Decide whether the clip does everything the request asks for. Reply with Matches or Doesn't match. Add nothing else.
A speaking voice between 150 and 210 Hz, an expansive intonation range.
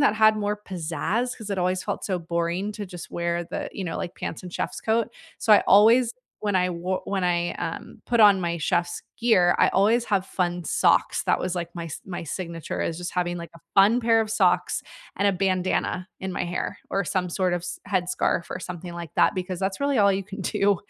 Doesn't match